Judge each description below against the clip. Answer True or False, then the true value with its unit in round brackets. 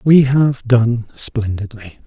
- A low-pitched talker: True (120 Hz)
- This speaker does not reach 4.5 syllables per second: True (3.3 syllables/s)